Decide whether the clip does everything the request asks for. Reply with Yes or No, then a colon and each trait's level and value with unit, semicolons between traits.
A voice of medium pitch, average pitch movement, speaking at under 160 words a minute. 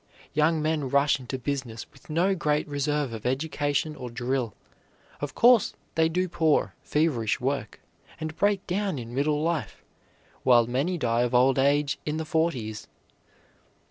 Yes: medium, 145 Hz; average, 4.1 semitones; average, 150 wpm